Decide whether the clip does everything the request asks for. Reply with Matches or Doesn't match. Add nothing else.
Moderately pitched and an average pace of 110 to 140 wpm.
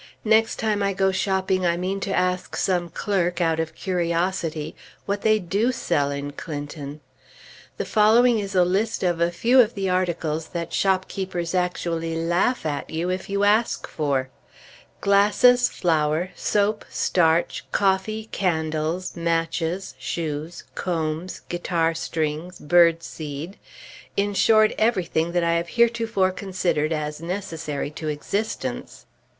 Matches